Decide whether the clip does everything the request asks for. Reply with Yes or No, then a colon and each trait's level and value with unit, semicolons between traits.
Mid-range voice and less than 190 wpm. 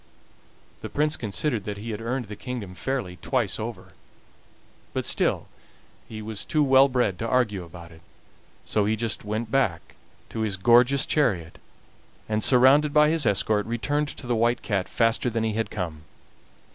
No: low, 115 Hz; average, 170 wpm